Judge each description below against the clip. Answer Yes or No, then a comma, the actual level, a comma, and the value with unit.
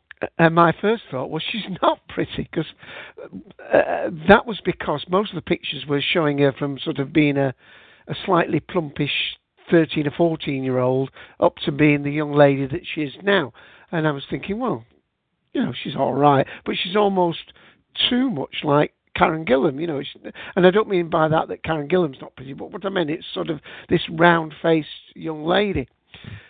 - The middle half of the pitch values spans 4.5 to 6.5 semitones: No, average, 3.9 semitones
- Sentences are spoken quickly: No, average, 195 wpm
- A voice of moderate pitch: Yes, medium, 160 Hz